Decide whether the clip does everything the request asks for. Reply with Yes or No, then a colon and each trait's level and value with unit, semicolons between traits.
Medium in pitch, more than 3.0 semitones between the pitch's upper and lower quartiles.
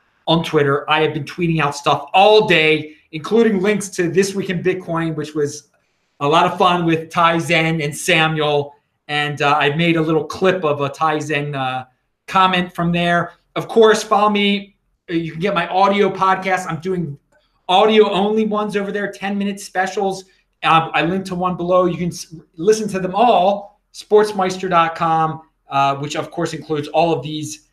Yes: medium, 170 Hz; average, 3.8 semitones